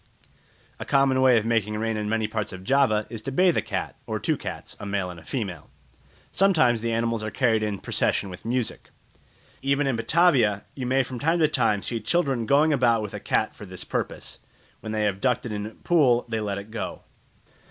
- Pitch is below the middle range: Yes, low, 115 Hz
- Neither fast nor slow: No, fast, 215 wpm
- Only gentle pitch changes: No, average, 4.0 semitones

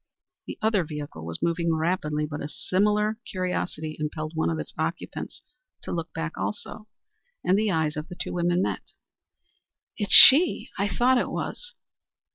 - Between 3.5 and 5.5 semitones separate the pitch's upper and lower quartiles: Yes, average, 5.0 semitones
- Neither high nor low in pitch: Yes, medium, 170 Hz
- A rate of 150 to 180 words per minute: Yes, average, 160 wpm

